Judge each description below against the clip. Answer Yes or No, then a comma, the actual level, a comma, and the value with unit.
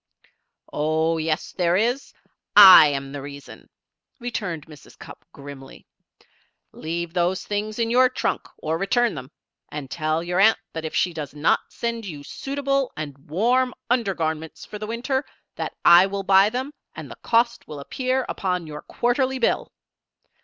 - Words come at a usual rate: Yes, average, 160 wpm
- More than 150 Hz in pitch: Yes, medium, 185 Hz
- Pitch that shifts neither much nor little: No, wide, 7.2 semitones